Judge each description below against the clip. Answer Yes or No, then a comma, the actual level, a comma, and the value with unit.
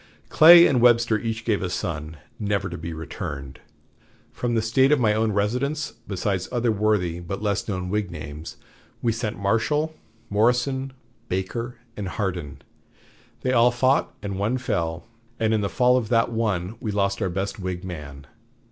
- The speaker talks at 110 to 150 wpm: No, average, 165 wpm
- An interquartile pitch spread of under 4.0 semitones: No, average, 4.6 semitones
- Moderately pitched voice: No, low, 105 Hz